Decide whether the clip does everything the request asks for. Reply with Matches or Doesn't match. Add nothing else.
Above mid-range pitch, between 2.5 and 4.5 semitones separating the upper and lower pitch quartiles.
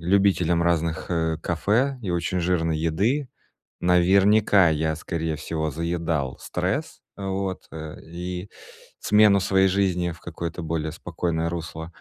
Doesn't match